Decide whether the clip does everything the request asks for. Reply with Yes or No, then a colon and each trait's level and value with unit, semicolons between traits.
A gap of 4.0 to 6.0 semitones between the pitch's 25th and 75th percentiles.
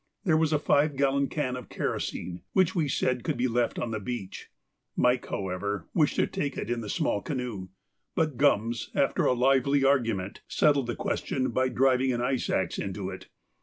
No: average, 3.6 semitones